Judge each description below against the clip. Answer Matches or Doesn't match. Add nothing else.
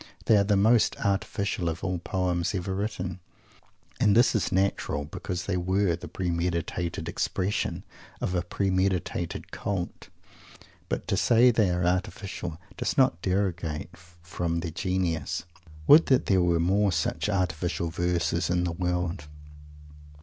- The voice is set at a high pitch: Doesn't match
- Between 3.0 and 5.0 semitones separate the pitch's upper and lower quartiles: Doesn't match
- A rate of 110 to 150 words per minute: Matches